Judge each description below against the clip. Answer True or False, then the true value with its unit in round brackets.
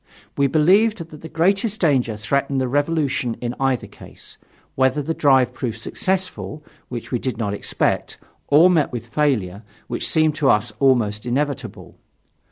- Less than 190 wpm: True (155 wpm)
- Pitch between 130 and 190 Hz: True (140 Hz)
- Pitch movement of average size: True (4.5 semitones)